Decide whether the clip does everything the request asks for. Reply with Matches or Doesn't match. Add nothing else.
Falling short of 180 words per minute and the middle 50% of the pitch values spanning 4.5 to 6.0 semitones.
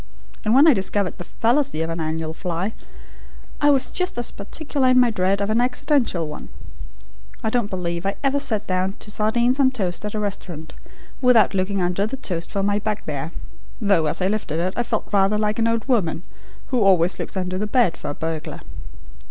Doesn't match